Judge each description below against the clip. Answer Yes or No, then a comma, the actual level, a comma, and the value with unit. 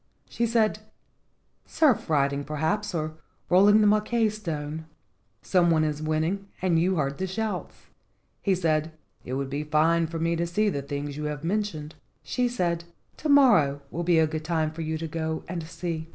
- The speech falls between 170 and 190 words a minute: Yes, average, 180 wpm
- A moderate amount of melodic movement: Yes, average, 4.0 semitones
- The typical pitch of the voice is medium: Yes, medium, 165 Hz